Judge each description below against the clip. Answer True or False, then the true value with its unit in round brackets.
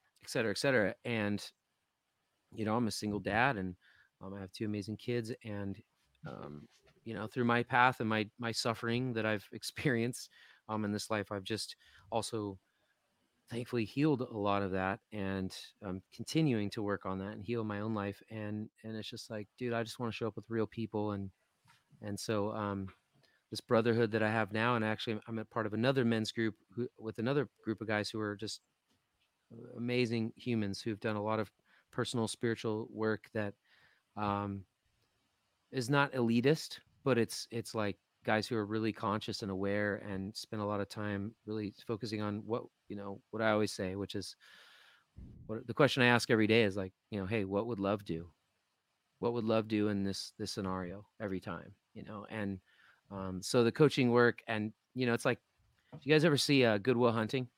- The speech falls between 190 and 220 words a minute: True (200 wpm)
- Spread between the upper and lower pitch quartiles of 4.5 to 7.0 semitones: False (2.5 semitones)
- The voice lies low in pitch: True (110 Hz)